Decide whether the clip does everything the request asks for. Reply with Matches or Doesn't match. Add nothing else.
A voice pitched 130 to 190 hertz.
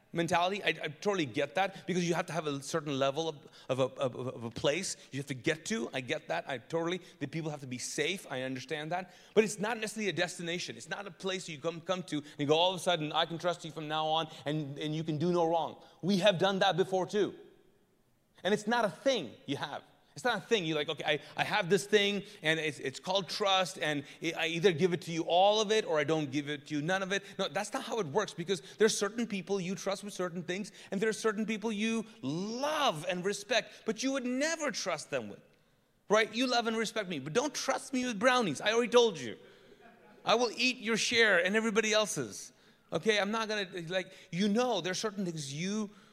Matches